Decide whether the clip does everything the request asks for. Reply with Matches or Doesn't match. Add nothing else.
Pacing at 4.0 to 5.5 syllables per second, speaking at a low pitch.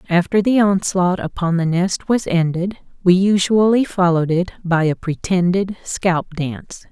Doesn't match